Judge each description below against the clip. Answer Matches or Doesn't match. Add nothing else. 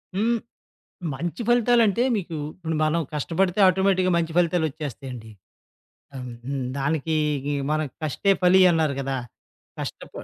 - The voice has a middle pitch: Matches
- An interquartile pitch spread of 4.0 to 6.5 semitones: Matches